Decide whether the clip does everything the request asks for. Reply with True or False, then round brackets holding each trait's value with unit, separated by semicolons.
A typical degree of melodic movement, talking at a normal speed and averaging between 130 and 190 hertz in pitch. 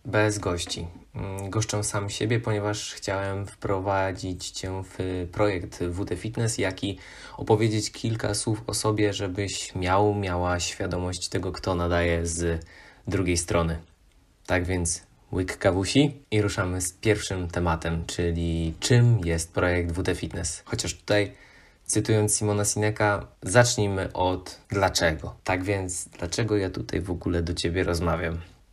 False (3.1 semitones; 130 wpm; 95 Hz)